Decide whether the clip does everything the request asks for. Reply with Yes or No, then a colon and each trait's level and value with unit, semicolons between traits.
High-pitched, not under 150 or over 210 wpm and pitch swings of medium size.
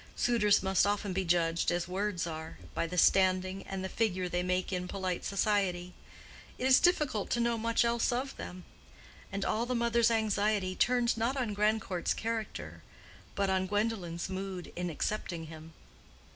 Yes: high, 195 Hz; average, 165 wpm; average, 3.8 semitones